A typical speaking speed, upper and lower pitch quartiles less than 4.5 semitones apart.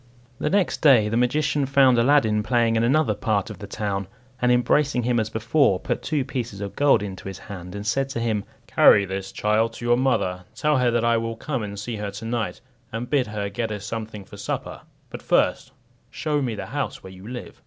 No: fast, 220 wpm; average, 3.6 semitones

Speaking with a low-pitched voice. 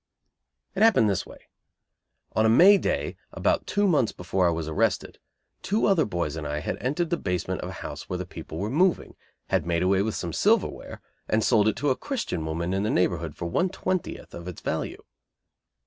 Yes: low, 100 Hz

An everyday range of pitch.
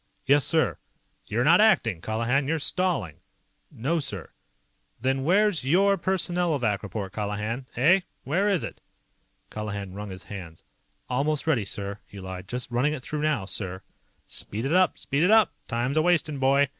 No: wide, 7.6 semitones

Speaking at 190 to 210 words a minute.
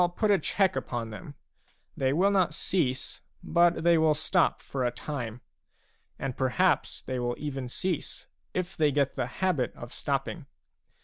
No: average, 160 wpm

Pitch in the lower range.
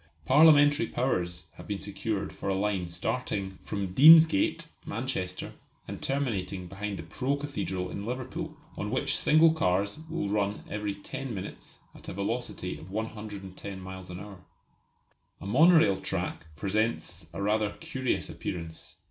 Yes: low, 100 Hz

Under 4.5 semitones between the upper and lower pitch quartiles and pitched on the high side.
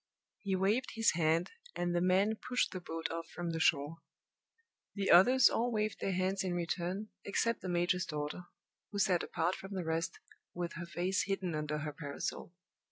No: average, 2.9 semitones; medium, 180 Hz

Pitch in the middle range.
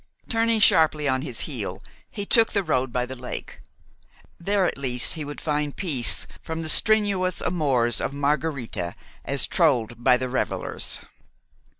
Yes: medium, 145 Hz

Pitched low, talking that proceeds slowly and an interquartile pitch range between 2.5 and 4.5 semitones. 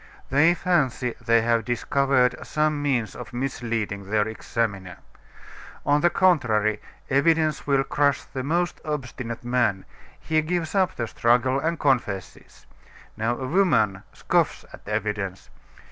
No: low, 125 Hz; slow, 130 wpm; average, 5.1 semitones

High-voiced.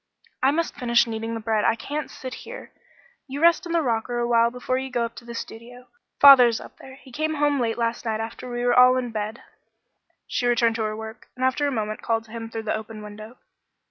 Yes: high, 240 Hz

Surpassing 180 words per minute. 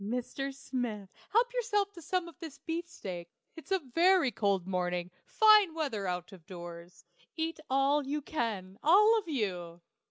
No: average, 155 wpm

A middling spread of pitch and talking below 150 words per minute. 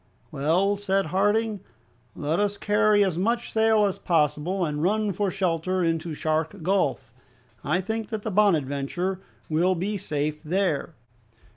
Yes: average, 4.5 semitones; average, 140 wpm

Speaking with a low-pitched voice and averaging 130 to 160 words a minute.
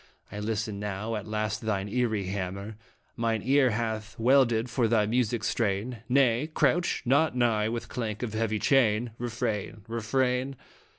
Yes: low, 115 Hz; average, 145 wpm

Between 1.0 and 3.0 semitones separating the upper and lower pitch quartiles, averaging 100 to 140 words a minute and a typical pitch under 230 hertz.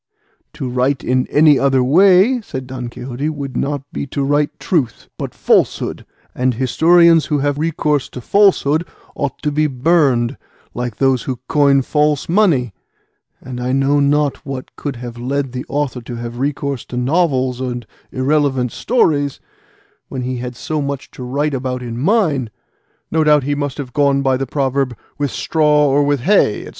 No: average, 2.7 semitones; average, 170 wpm; medium, 140 Hz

